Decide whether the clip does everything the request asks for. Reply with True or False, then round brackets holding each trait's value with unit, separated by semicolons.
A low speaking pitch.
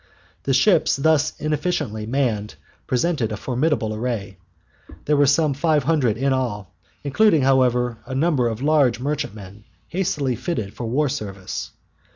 True (130 Hz)